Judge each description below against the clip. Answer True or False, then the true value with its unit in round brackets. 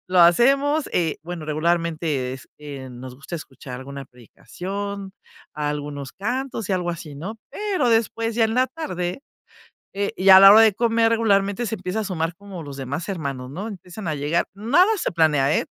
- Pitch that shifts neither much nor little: False (6.8 semitones)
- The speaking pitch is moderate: True (180 Hz)